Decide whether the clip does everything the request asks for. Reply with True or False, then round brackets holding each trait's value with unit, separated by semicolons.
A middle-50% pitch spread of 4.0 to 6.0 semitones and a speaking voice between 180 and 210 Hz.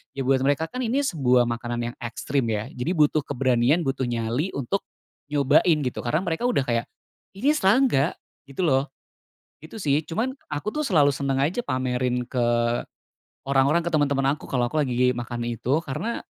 False (4.3 semitones; 140 Hz)